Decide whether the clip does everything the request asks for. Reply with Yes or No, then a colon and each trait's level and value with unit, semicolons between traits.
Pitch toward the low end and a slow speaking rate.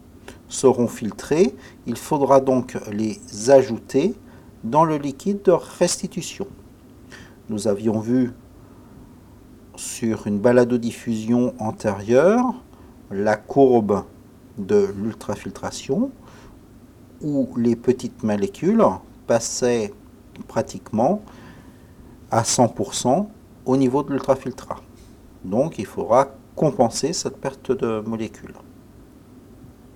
Yes: low, 125 Hz; slow, 90 wpm